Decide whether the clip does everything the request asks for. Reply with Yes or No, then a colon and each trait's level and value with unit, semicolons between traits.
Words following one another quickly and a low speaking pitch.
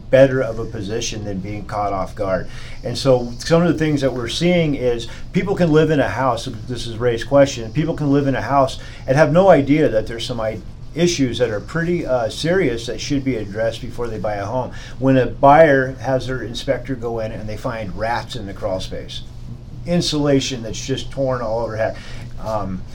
Yes: fast, 210 wpm; low, 125 Hz